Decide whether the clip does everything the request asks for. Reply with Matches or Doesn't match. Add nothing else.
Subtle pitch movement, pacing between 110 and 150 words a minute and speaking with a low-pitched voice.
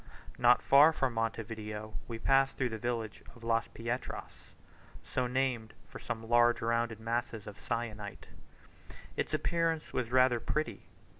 Matches